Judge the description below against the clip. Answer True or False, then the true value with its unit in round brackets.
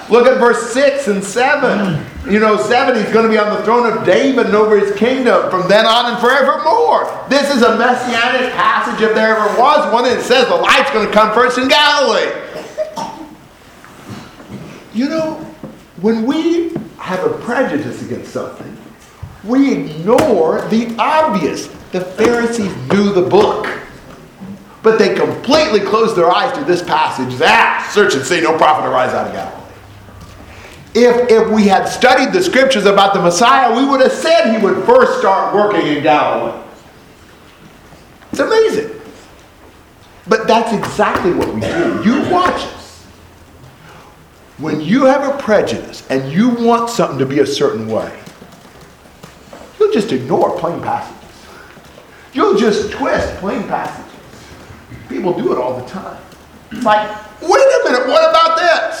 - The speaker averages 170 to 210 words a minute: False (155 wpm)